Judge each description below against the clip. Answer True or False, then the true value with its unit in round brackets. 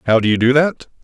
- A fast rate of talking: True (290 wpm)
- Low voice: True (130 Hz)